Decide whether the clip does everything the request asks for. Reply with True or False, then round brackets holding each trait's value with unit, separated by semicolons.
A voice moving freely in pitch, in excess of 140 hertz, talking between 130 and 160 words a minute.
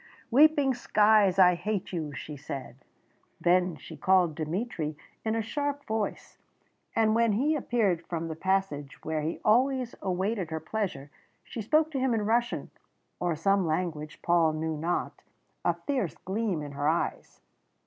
True (5.9 semitones; 190 Hz; 155 wpm)